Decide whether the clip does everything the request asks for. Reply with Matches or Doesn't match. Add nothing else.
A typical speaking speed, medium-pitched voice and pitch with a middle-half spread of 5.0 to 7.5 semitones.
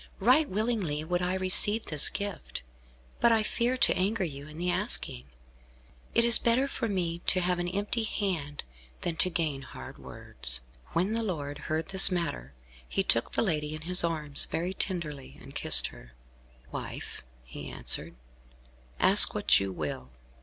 Matches